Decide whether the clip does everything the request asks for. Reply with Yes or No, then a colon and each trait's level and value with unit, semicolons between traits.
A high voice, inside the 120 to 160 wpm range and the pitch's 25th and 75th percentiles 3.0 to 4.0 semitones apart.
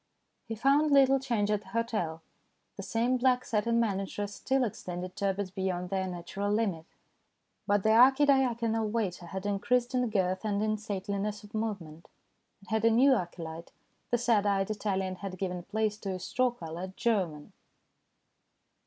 Yes: high, 205 Hz; average, 155 wpm; average, 3.6 semitones